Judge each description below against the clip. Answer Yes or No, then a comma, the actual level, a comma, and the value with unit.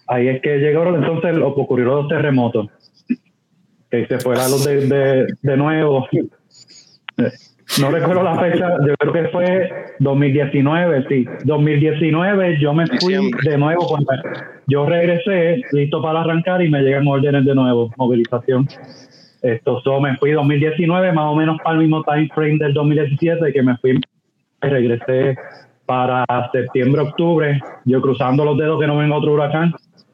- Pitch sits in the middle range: Yes, medium, 145 Hz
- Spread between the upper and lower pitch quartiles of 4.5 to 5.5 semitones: No, average, 3.5 semitones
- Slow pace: No, average, 150 wpm